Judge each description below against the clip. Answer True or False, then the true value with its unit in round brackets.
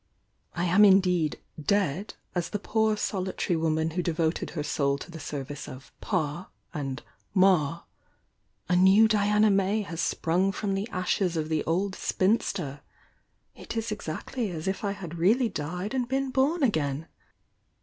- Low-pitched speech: False (185 Hz)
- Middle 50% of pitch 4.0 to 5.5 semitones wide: True (4.5 semitones)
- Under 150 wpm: False (160 wpm)